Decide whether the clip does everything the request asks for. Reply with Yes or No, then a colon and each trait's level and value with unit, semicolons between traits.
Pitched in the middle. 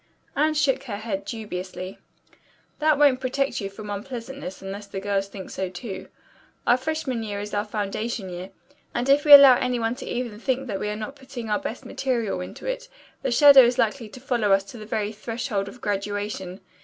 No: high, 225 Hz